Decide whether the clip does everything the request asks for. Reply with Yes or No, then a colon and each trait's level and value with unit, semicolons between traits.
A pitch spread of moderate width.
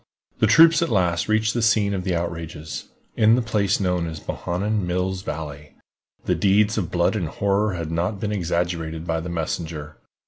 Yes: average, 4.0 semitones